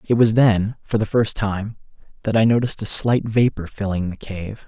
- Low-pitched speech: Yes, low, 110 Hz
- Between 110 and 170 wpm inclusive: No, fast, 205 wpm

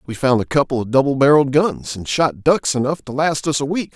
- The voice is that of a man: Yes, male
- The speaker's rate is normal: No, fast, 260 wpm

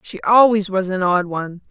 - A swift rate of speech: Yes, fast, 210 wpm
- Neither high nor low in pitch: No, high, 195 Hz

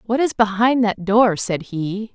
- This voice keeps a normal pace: Yes, average, 195 wpm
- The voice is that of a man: No, female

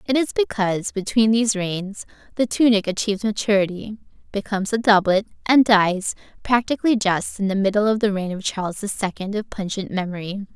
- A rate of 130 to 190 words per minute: Yes, average, 170 wpm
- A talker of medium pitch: No, high, 205 Hz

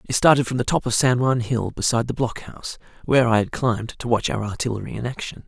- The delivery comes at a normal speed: No, fast, 250 wpm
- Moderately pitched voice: No, low, 120 Hz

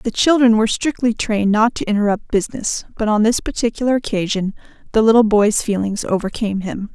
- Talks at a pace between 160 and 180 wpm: Yes, average, 175 wpm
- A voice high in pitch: Yes, high, 220 Hz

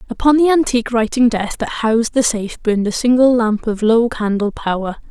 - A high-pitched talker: Yes, high, 230 Hz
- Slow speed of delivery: No, average, 200 wpm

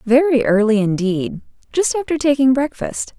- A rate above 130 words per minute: No, slow, 115 wpm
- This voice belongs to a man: No, female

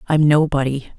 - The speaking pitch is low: No, medium, 145 Hz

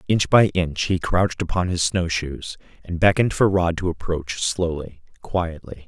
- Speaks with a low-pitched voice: Yes, very low, 85 Hz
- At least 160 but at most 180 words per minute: Yes, average, 175 wpm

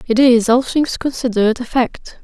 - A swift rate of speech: No, average, 190 wpm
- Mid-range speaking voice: No, high, 245 Hz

